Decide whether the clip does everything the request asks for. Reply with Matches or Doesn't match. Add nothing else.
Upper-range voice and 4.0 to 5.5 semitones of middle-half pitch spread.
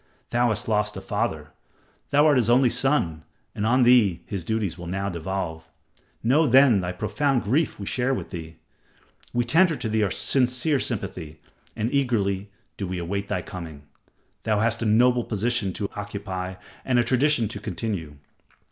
Doesn't match